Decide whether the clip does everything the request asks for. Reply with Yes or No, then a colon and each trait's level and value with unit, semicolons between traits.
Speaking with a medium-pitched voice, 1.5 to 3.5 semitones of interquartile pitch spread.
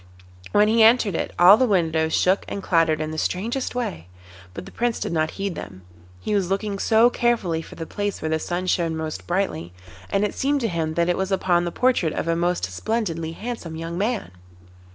No: medium, 180 Hz; average, 4.7 semitones